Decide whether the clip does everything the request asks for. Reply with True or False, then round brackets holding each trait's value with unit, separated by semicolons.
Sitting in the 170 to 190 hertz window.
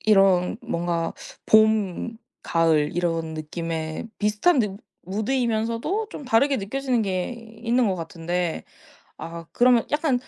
False (205 Hz)